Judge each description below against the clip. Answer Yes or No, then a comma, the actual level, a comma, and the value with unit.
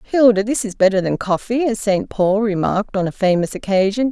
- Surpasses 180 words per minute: Yes, fast, 205 wpm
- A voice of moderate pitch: No, high, 205 Hz